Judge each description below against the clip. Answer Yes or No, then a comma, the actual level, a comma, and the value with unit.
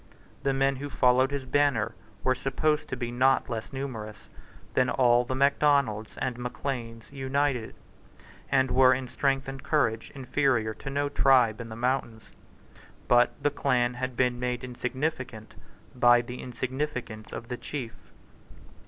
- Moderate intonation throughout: No, narrow, 2.0 semitones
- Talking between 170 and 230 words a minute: No, average, 145 wpm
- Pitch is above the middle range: No, low, 130 Hz